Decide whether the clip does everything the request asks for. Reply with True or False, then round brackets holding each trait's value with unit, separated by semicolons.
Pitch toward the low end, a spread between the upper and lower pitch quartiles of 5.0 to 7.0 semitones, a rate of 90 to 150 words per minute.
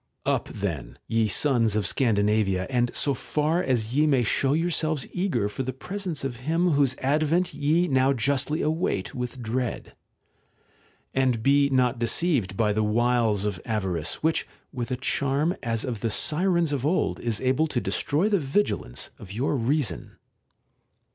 False (130 Hz; 5.3 semitones; 160 wpm)